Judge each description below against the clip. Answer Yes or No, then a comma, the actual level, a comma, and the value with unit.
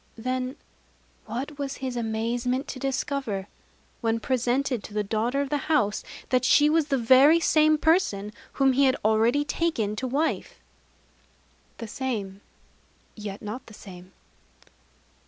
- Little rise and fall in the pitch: No, average, 4.2 semitones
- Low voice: No, very high, 255 Hz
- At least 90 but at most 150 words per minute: Yes, average, 140 wpm